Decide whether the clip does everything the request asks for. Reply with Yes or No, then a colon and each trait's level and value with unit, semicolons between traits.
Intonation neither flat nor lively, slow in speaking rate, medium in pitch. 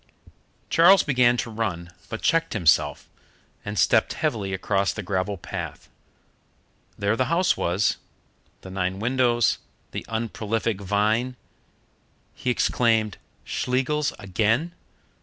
No: average, 4.1 semitones; slow, 110 wpm; low, 110 Hz